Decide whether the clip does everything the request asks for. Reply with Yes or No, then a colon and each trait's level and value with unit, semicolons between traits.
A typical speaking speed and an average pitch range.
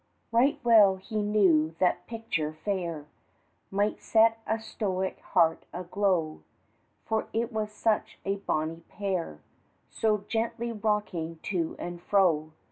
No: slow, 125 wpm; average, 4.4 semitones